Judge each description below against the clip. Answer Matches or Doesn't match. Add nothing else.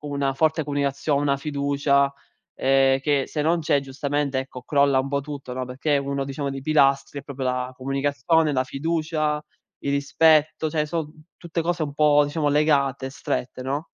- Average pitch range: Doesn't match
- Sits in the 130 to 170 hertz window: Matches